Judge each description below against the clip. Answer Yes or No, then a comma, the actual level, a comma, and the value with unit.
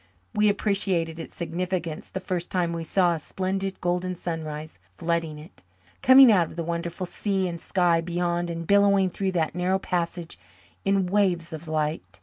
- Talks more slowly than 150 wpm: No, average, 165 wpm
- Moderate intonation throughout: No, narrow, 2.3 semitones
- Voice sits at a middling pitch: Yes, medium, 175 Hz